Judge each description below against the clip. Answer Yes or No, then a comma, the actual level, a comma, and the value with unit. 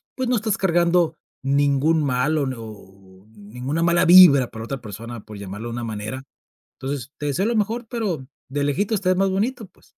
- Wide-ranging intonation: Yes, wide, 7.8 semitones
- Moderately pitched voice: Yes, medium, 145 Hz